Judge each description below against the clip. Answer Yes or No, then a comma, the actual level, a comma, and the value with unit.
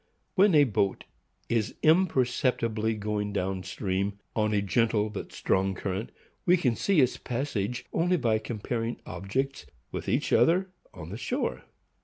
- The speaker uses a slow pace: No, average, 145 wpm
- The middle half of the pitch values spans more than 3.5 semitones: Yes, average, 5.1 semitones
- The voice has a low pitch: Yes, low, 115 Hz